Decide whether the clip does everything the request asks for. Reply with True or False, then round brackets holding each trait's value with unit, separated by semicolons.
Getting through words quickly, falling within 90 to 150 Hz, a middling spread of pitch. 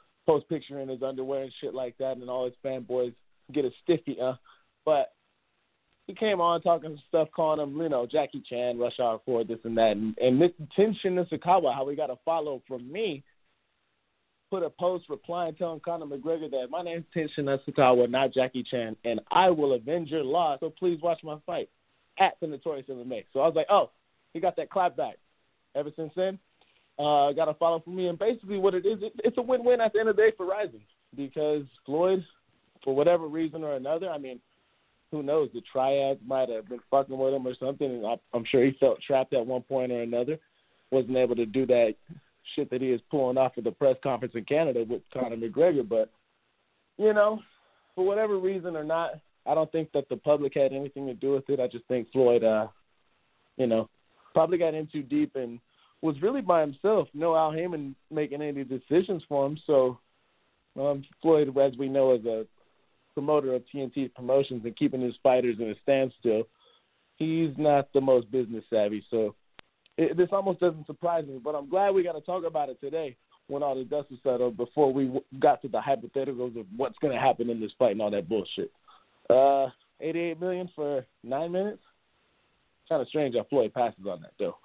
True (210 wpm; 140 Hz; 4.5 semitones)